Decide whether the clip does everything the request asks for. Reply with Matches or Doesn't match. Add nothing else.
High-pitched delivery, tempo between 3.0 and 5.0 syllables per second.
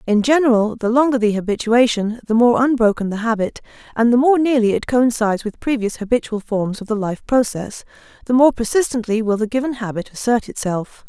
Doesn't match